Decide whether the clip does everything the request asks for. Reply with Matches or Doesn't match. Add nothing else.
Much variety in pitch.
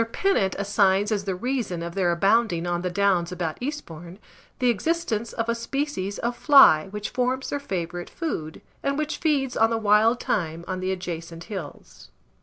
Matches